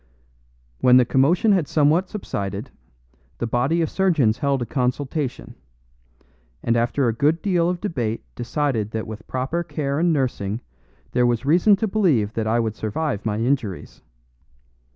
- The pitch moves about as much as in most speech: No, wide, 6.1 semitones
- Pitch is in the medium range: No, low, 130 Hz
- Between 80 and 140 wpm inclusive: No, average, 150 wpm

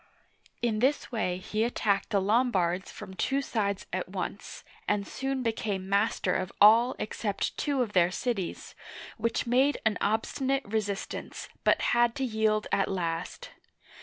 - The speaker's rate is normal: Yes, average, 145 wpm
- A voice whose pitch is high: Yes, high, 215 Hz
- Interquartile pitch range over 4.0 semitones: No, average, 3.7 semitones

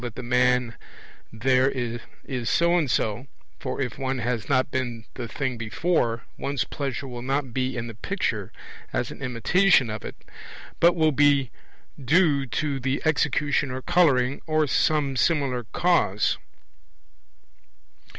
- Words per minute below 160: Yes, average, 140 wpm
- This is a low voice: Yes, low, 130 Hz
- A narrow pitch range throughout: No, average, 3.2 semitones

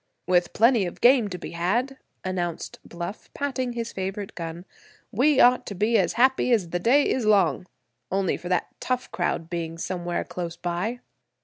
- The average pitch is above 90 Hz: Yes, high, 190 Hz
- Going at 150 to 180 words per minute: Yes, average, 170 wpm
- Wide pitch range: Yes, wide, 5.7 semitones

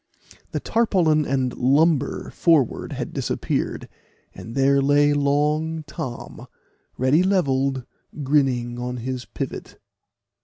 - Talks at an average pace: No, slow, 105 wpm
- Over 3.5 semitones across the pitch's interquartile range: No, average, 2.9 semitones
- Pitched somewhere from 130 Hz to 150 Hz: Yes, medium, 140 Hz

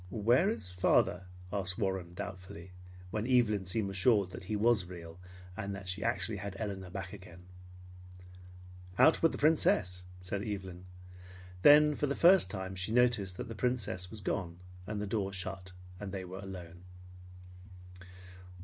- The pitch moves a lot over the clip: No, average, 3.1 semitones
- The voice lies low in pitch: Yes, low, 100 Hz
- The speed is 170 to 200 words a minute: No, average, 155 wpm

